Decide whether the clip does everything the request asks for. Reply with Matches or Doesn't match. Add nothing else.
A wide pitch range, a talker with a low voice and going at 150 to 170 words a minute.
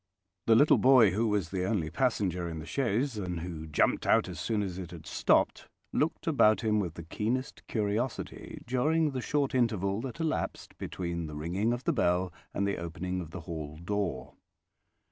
Doesn't match